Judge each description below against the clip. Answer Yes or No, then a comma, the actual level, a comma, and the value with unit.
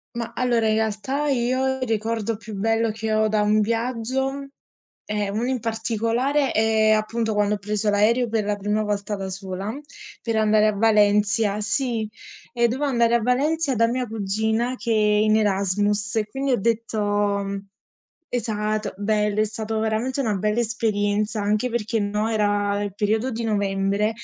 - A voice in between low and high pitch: No, high, 220 Hz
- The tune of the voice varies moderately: No, narrow, 1.9 semitones